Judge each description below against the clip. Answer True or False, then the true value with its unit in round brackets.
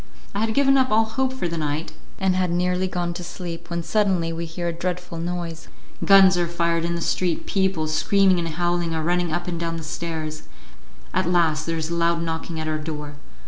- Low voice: False (170 Hz)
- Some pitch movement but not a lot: False (1.7 semitones)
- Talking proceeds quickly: True (220 wpm)